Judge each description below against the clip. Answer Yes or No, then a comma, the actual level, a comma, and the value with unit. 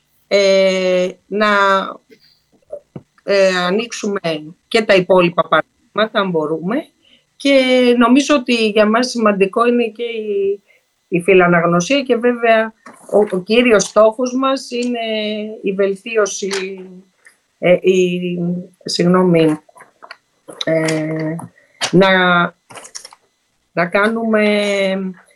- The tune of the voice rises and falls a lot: No, average, 3.9 semitones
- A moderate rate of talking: No, slow, 90 wpm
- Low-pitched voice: No, high, 200 Hz